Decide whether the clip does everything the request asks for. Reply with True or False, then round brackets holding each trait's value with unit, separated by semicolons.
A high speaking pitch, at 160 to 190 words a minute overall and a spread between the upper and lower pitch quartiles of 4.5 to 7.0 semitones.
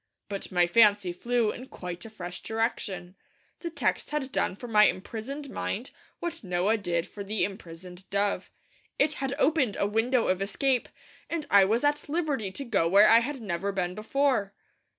True (215 Hz; 175 wpm; 5.5 semitones)